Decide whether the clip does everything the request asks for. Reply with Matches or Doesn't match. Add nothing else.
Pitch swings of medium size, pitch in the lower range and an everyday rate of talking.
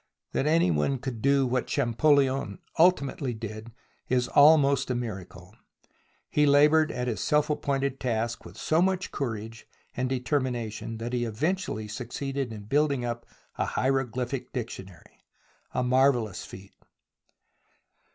Doesn't match